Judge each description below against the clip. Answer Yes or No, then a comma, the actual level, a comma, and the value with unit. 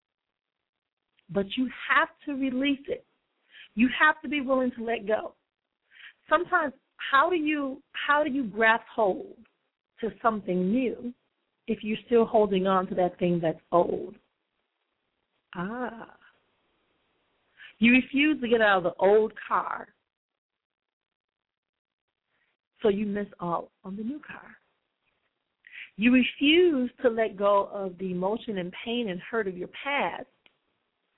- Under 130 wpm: No, slow, 135 wpm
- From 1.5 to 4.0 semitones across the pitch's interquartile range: No, wide, 5.4 semitones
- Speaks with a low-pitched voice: No, high, 230 Hz